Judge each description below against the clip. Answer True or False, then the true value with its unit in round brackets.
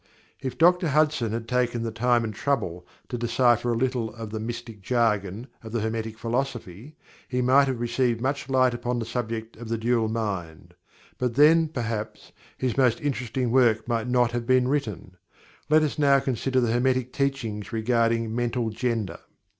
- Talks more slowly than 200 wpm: True (170 wpm)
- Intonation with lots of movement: False (2.4 semitones)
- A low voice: True (120 Hz)